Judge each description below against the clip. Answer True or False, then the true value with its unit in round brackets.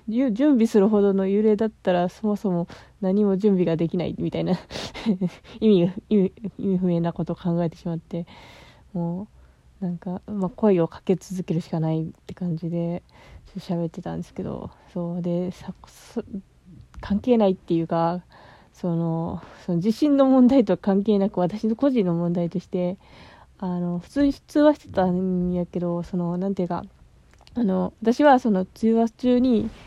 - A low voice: False (185 Hz)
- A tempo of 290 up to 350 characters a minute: True (300 characters per minute)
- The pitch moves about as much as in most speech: True (3.5 semitones)